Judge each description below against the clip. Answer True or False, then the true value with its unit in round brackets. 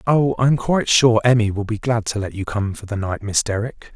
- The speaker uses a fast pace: True (260 wpm)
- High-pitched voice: False (115 Hz)